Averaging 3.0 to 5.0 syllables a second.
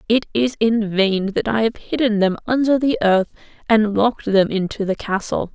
Yes: 4.8 syllables/s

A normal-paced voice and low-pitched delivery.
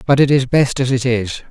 No: fast, 280 wpm; low, 130 Hz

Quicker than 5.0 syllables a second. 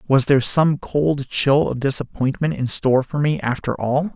No: 4.8 syllables/s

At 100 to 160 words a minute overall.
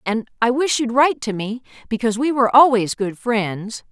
No: average, 200 wpm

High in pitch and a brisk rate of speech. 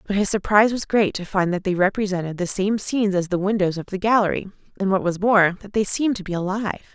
Yes: high, 195 Hz; fast, 250 wpm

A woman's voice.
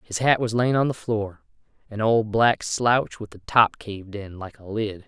No: male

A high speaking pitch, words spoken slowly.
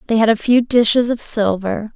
No: high, 225 Hz; fast, 215 wpm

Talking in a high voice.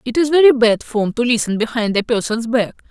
Yes: high, 235 Hz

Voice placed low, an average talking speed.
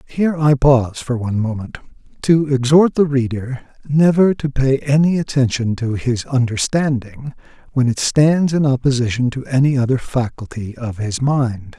Yes: low, 130 Hz; average, 155 wpm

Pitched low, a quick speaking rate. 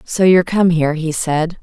No: medium, 170 Hz; fast, 220 wpm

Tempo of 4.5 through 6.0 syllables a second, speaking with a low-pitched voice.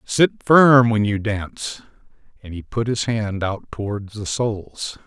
No: 4.0 syllables/s; low, 110 Hz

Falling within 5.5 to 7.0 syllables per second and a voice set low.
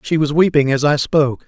No: 5.8 syllables/s; medium, 145 Hz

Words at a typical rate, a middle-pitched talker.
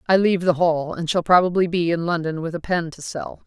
No: fast, 260 wpm; medium, 170 Hz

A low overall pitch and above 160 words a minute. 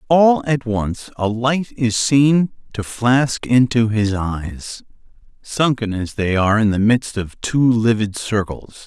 No: low, 115 Hz; average, 150 wpm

